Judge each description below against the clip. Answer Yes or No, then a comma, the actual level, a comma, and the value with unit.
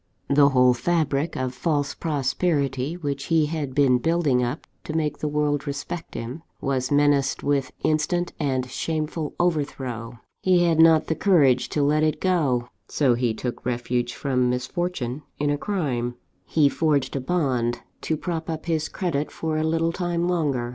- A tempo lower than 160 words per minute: No, average, 165 wpm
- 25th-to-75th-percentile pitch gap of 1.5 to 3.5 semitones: No, average, 4.0 semitones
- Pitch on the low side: No, medium, 145 Hz